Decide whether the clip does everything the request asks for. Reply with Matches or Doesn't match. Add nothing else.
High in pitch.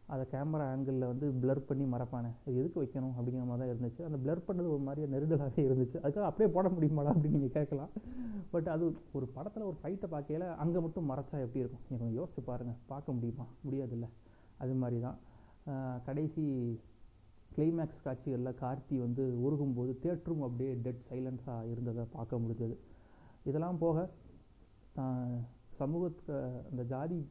Doesn't match